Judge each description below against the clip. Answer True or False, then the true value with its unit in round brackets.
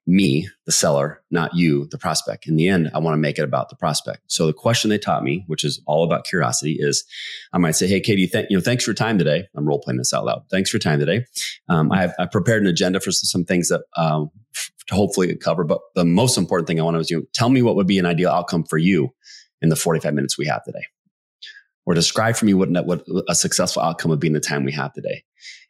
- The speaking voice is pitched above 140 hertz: False (85 Hz)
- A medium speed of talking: False (265 wpm)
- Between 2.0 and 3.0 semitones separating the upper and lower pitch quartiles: False (4.1 semitones)